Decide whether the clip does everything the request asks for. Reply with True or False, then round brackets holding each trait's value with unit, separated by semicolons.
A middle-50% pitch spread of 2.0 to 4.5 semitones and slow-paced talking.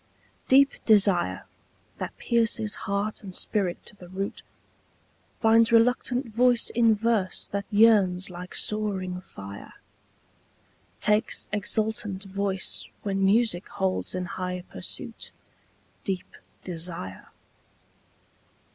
True (3.3 semitones; 100 wpm)